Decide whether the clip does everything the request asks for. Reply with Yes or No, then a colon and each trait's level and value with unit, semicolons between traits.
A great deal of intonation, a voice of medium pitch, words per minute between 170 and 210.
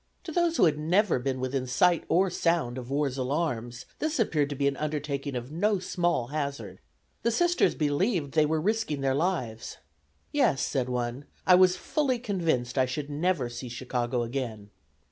Yes: wide, 5.9 semitones; medium, 145 Hz; average, 175 wpm